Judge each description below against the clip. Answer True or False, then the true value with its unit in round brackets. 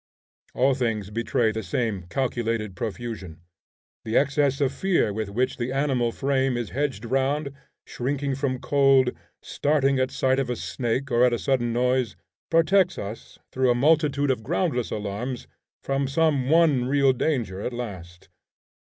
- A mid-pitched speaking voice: False (130 Hz)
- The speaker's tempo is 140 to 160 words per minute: True (155 wpm)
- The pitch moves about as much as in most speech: True (3.2 semitones)